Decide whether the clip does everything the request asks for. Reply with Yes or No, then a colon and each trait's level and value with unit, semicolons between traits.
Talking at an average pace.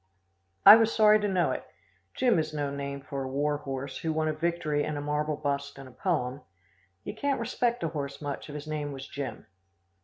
No: fast, 215 wpm